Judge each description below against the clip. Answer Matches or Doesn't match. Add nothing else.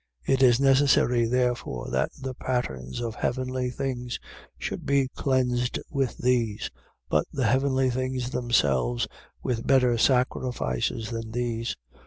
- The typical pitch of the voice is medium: Doesn't match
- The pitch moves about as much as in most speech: Doesn't match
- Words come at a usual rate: Doesn't match